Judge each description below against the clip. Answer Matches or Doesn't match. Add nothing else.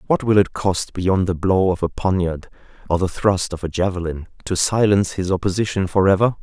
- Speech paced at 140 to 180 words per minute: Doesn't match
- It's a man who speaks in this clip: Matches